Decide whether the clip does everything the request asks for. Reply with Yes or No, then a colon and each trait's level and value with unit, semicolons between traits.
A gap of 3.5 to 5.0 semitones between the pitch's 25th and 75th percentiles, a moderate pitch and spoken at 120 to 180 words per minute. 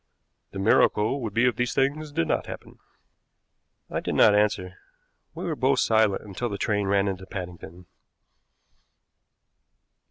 No: average, 4.2 semitones; low, 105 Hz; average, 145 wpm